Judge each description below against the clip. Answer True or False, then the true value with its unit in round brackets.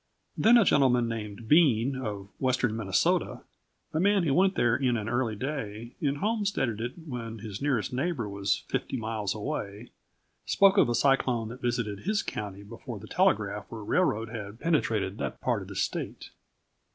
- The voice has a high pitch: False (120 Hz)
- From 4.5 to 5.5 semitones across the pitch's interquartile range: True (4.9 semitones)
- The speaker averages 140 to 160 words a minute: False (170 wpm)